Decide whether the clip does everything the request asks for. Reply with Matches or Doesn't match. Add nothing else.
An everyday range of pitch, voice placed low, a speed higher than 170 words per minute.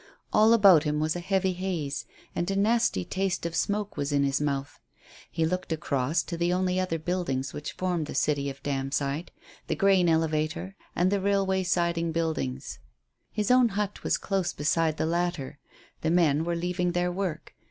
Doesn't match